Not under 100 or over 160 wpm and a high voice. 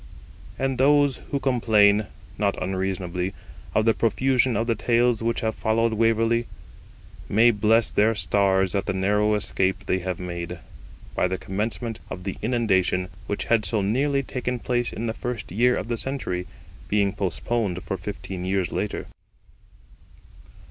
No: average, 155 wpm; low, 105 Hz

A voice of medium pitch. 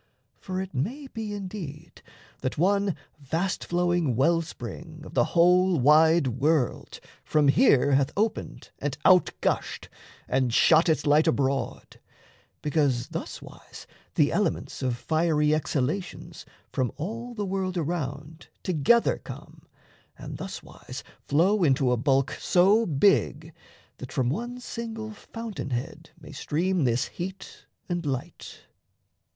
Yes: medium, 160 Hz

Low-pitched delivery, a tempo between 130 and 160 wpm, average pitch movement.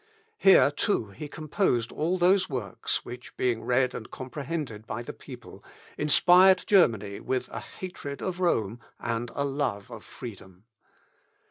No: low, 130 Hz; average, 140 wpm; wide, 6.6 semitones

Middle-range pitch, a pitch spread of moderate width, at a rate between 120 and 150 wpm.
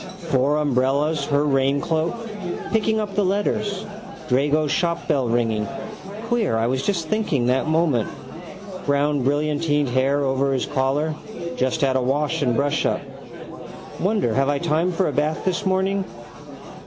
Yes: medium, 145 Hz; average, 4.2 semitones; average, 140 wpm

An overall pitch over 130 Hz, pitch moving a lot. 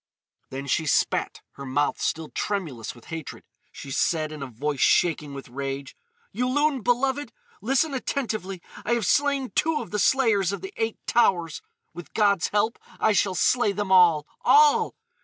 Yes: high, 190 Hz; wide, 8.3 semitones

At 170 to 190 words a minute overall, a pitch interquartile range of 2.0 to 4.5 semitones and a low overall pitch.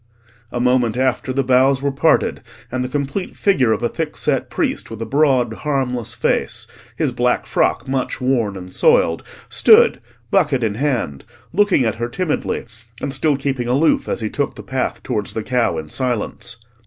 Yes: average, 175 wpm; average, 2.9 semitones; low, 130 Hz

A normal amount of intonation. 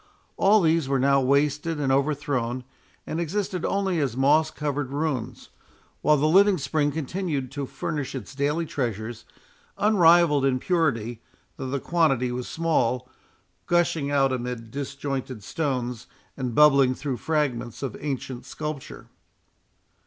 Yes: average, 3.5 semitones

